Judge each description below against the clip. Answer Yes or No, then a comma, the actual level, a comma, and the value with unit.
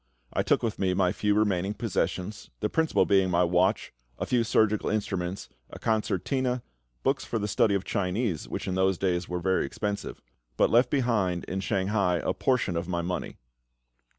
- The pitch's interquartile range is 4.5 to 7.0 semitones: No, average, 3.3 semitones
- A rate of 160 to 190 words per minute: Yes, average, 180 wpm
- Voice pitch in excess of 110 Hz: No, low, 100 Hz